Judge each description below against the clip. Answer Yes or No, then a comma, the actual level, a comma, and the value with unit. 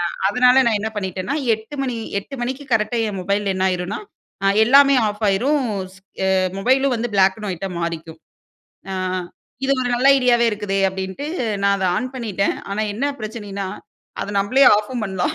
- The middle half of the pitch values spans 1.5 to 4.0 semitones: No, average, 4.4 semitones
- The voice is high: Yes, high, 210 Hz